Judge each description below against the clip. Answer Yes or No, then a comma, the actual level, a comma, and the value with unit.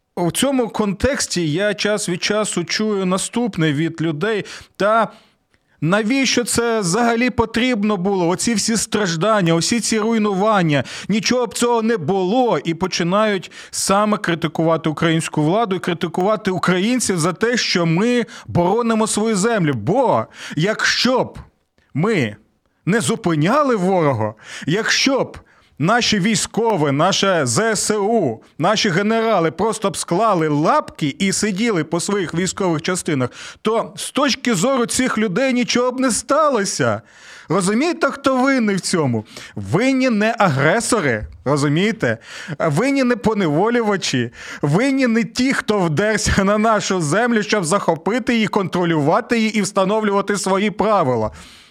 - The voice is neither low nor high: No, high, 205 Hz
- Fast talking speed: No, average, 125 wpm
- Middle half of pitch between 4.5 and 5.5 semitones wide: Yes, average, 5.0 semitones